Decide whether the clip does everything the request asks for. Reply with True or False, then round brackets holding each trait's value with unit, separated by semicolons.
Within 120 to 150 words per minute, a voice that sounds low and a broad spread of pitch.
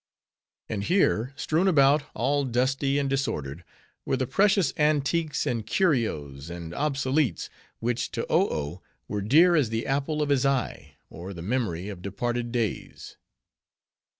True (145 wpm; 130 Hz; 6.0 semitones)